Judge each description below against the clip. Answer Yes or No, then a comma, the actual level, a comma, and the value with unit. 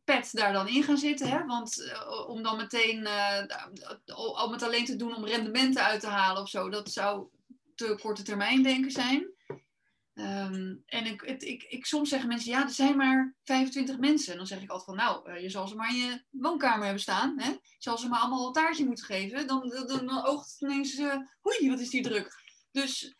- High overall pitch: Yes, very high, 250 Hz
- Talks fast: Yes, fast, 220 wpm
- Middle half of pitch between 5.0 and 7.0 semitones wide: No, average, 4.2 semitones